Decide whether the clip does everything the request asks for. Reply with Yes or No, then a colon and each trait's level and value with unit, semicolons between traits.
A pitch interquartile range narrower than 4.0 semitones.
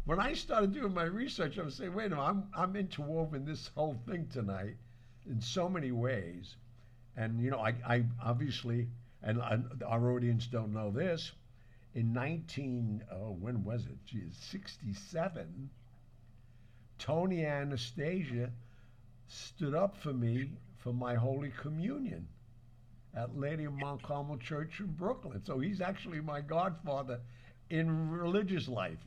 No: average, 5.3 semitones